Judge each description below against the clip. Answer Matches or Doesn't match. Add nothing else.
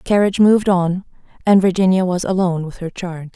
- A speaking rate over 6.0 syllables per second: Matches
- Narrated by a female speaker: Matches